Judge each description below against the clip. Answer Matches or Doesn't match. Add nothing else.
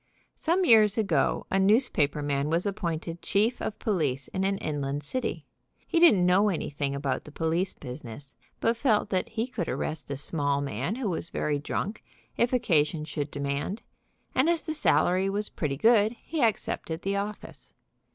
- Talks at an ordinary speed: Matches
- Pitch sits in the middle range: Matches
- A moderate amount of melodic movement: Doesn't match